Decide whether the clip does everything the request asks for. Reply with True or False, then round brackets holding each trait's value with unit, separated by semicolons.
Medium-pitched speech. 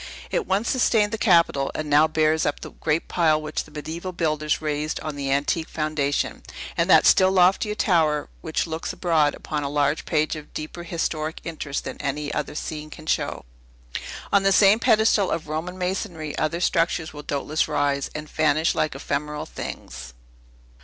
True (155 Hz)